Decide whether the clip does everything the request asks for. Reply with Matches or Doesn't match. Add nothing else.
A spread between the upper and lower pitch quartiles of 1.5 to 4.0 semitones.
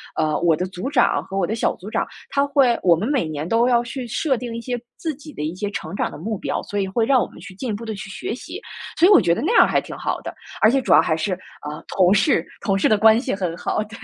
Doesn't match